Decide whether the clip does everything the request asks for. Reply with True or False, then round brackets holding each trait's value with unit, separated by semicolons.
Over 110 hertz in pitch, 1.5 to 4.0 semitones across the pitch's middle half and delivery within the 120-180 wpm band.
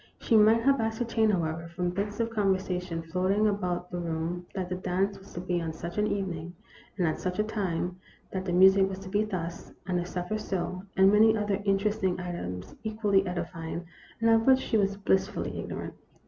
False (190 Hz; 2.9 semitones; 200 wpm)